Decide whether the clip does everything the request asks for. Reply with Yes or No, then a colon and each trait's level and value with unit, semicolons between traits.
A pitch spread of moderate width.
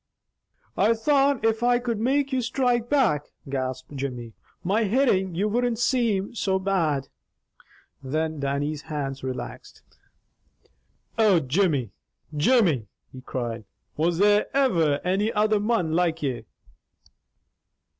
No: wide, 8.3 semitones